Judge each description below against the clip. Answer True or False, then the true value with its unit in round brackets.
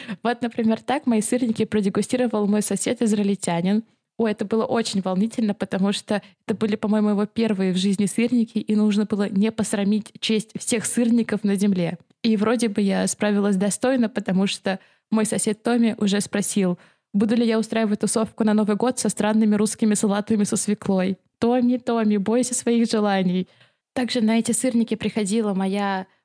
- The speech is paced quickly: True (165 wpm)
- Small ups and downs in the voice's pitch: True (2.1 semitones)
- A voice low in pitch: False (215 Hz)